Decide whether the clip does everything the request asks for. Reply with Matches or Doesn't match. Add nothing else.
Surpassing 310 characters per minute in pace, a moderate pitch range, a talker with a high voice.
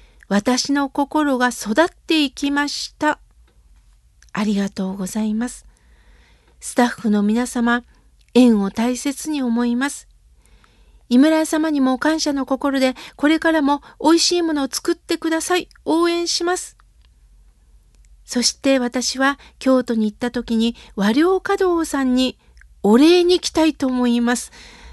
Doesn't match